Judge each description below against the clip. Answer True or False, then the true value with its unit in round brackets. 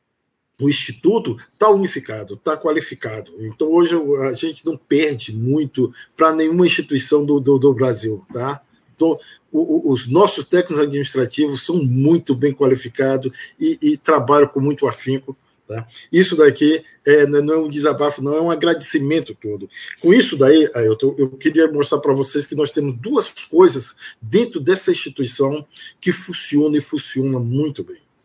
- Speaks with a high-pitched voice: False (145 Hz)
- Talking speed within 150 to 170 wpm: True (160 wpm)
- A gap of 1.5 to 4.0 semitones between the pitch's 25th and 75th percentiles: True (3.0 semitones)